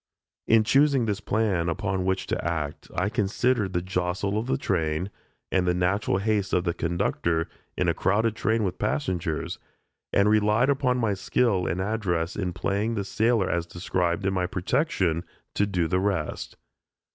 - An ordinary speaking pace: Yes, average, 170 wpm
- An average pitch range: Yes, average, 3.5 semitones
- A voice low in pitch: Yes, very low, 95 Hz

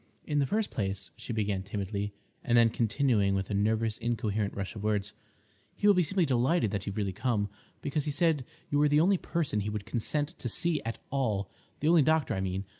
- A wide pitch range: Yes, wide, 6.4 semitones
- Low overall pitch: Yes, low, 115 Hz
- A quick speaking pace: Yes, fast, 210 wpm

